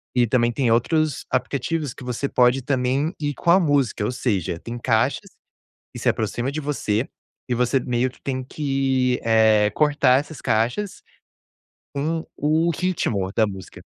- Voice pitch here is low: Yes, low, 130 Hz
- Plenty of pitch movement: No, average, 3.7 semitones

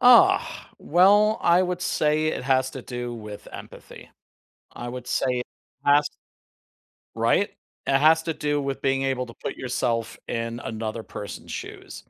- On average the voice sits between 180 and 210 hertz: No, low, 135 Hz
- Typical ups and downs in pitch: Yes, average, 4.5 semitones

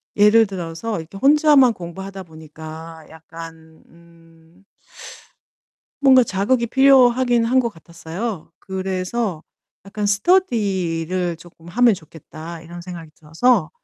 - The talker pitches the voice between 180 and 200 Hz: Yes, medium, 185 Hz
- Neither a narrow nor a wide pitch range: No, wide, 5.9 semitones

